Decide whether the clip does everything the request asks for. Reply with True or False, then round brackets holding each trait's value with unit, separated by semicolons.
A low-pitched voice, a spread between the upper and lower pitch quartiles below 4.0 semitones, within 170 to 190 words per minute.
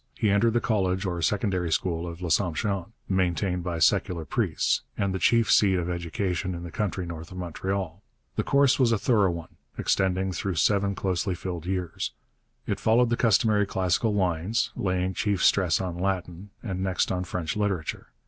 True (95 Hz; 2.5 semitones; 175 wpm)